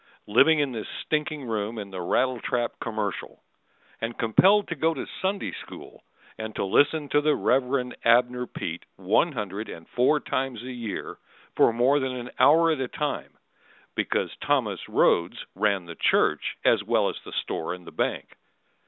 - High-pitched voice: No, low, 125 Hz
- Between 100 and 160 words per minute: No, average, 170 wpm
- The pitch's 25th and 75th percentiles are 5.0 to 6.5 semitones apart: Yes, average, 5.3 semitones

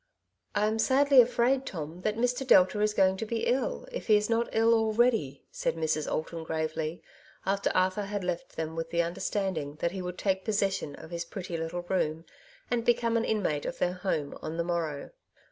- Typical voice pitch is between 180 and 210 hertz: Yes, high, 190 Hz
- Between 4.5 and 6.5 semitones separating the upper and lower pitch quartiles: Yes, average, 5.3 semitones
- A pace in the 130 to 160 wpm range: No, fast, 205 wpm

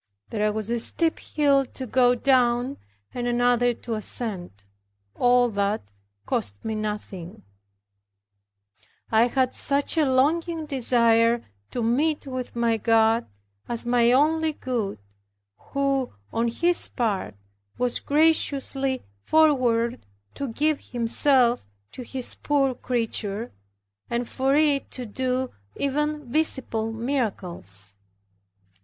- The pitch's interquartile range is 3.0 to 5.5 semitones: Yes, average, 3.4 semitones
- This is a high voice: Yes, high, 245 Hz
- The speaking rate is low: Yes, slow, 110 wpm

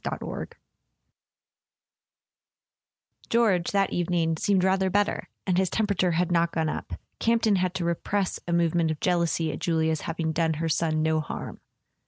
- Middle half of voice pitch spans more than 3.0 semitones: No, average, 2.7 semitones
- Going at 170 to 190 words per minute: No, average, 155 wpm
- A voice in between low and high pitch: Yes, medium, 170 Hz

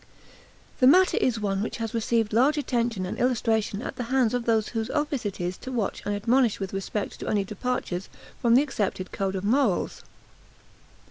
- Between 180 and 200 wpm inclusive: Yes, average, 190 wpm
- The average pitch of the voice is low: No, high, 225 Hz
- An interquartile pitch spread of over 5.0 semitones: No, average, 3.8 semitones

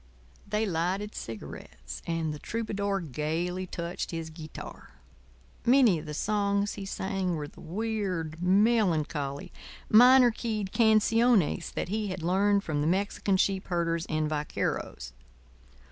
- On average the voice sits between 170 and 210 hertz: Yes, medium, 185 Hz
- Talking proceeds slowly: Yes, slow, 130 wpm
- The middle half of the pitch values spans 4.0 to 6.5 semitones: Yes, average, 4.6 semitones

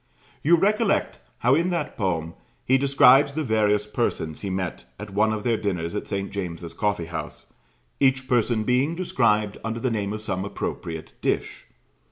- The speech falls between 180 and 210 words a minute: No, average, 170 wpm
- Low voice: Yes, low, 110 Hz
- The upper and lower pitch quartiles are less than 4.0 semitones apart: No, average, 4.9 semitones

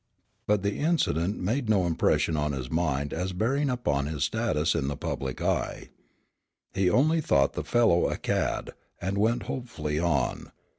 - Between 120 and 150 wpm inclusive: No, average, 160 wpm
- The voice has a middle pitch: No, very low, 90 Hz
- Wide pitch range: Yes, wide, 7.4 semitones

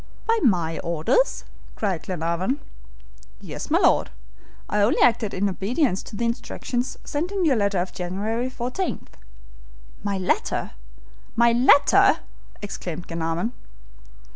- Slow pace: Yes, slow, 120 wpm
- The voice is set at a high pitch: Yes, high, 210 Hz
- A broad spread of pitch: Yes, wide, 5.8 semitones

